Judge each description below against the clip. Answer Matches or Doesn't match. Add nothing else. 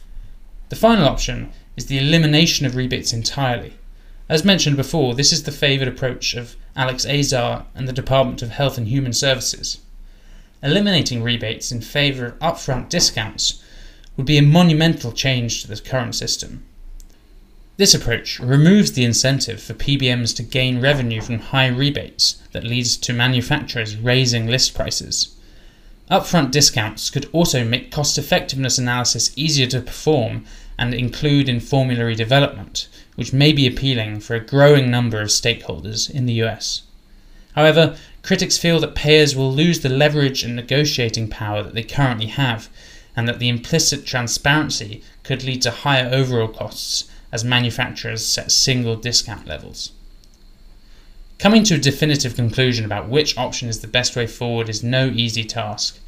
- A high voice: Doesn't match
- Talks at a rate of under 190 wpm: Matches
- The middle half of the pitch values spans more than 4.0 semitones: Doesn't match